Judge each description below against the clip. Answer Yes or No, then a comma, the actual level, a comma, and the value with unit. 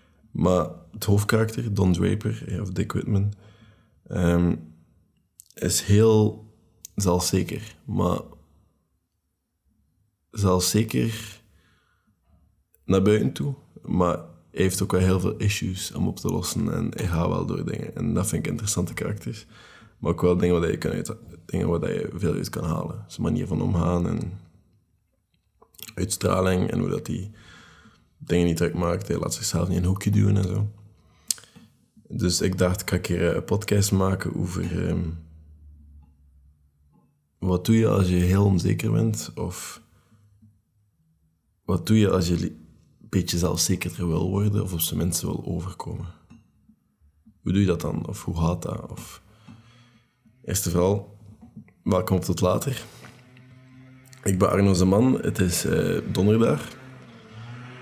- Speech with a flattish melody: No, average, 3.8 semitones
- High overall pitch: No, very low, 95 Hz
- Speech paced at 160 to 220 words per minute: No, average, 145 wpm